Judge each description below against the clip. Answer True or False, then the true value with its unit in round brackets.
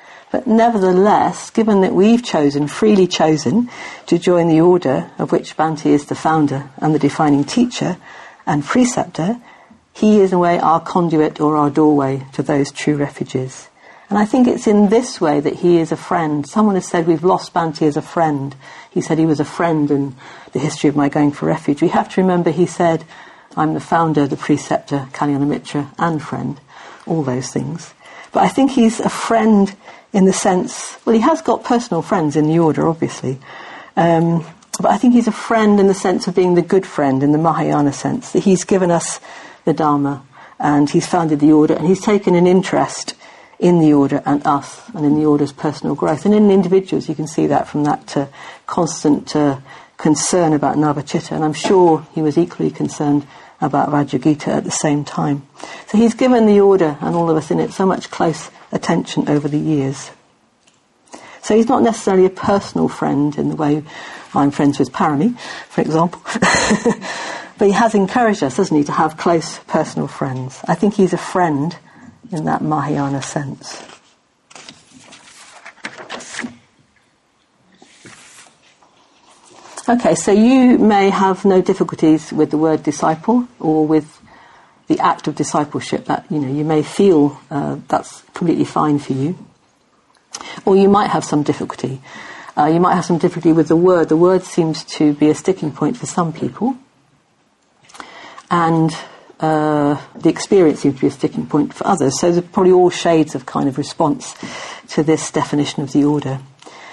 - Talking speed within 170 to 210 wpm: True (180 wpm)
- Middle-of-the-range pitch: True (165 Hz)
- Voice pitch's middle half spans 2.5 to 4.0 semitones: False (4.4 semitones)